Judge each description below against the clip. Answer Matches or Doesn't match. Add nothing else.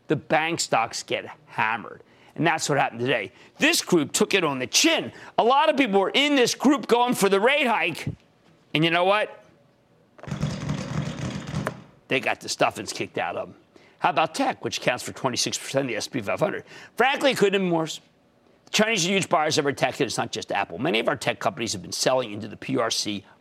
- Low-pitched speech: Doesn't match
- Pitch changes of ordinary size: Doesn't match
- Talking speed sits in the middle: Doesn't match